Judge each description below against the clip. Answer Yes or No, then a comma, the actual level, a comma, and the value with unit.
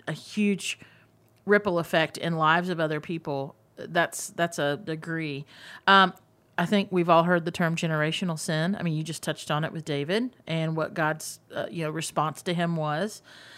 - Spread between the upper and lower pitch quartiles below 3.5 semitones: Yes, narrow, 2.4 semitones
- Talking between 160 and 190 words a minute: Yes, average, 185 wpm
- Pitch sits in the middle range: Yes, medium, 160 Hz